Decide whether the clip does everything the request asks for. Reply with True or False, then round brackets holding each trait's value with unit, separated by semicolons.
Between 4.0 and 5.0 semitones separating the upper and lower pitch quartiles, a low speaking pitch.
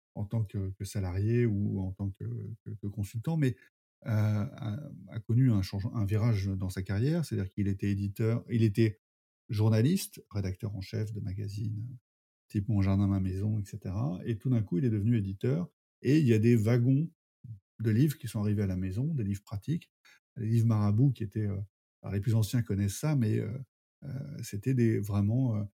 False (3.1 semitones; 110 Hz)